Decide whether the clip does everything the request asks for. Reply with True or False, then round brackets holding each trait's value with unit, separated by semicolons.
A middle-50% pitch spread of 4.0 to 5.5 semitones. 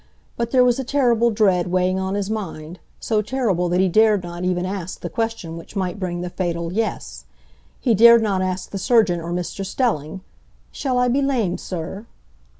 True (4.3 semitones)